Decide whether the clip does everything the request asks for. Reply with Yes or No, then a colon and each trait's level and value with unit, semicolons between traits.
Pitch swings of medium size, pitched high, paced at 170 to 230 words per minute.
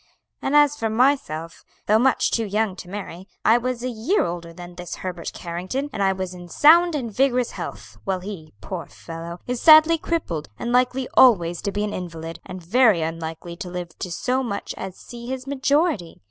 No: wide, 6.6 semitones; high, 205 Hz; average, 195 wpm